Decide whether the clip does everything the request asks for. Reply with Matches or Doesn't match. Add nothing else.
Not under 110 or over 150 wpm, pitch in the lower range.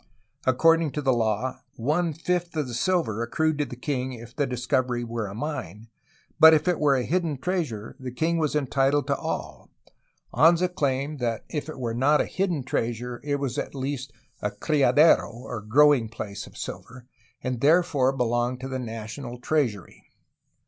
Doesn't match